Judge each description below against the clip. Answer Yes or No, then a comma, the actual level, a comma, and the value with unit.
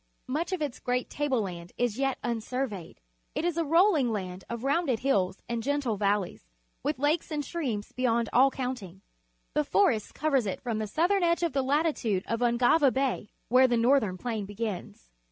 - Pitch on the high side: Yes, very high, 250 Hz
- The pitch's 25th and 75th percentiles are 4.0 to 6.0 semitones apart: Yes, average, 5.2 semitones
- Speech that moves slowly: No, average, 190 wpm